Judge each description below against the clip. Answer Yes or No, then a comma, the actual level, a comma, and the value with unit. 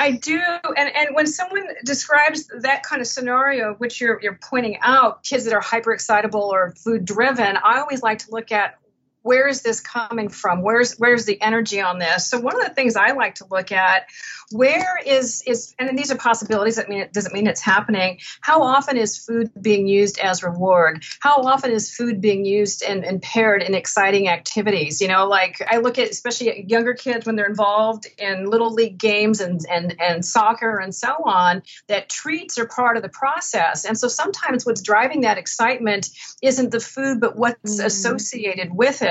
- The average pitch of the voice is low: No, high, 225 Hz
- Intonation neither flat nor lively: Yes, average, 4.1 semitones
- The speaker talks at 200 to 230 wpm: Yes, fast, 205 wpm